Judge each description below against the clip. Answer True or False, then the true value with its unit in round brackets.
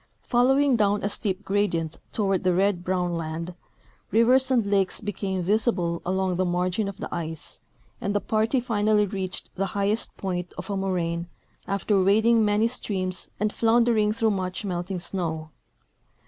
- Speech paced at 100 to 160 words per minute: True (155 wpm)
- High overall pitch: True (195 Hz)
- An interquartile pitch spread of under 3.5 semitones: True (3.0 semitones)